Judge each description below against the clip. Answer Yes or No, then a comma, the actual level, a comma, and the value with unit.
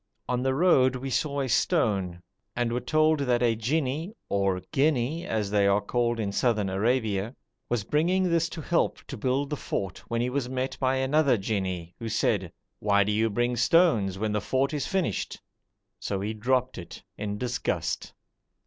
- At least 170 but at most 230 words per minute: Yes, average, 180 wpm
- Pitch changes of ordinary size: Yes, average, 4.9 semitones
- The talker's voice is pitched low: Yes, low, 120 Hz